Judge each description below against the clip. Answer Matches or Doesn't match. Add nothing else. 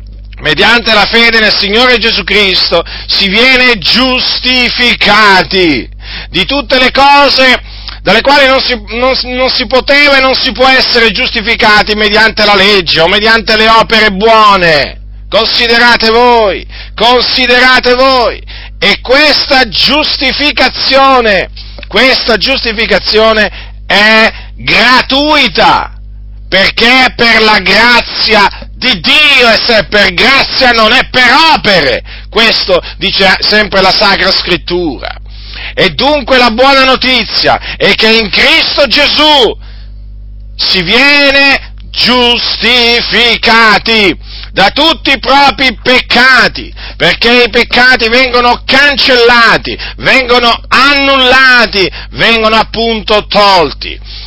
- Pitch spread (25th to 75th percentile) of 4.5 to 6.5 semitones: Doesn't match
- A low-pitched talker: Doesn't match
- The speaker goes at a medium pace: Doesn't match